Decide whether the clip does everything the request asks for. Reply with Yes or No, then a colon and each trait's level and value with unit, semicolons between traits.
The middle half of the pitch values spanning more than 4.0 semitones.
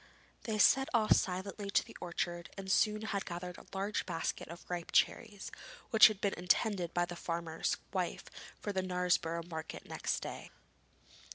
No: average, 3.0 semitones